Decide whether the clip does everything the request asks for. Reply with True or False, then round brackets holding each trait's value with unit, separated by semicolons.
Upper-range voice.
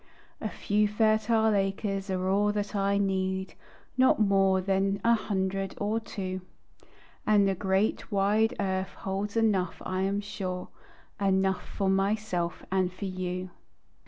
True (195 Hz)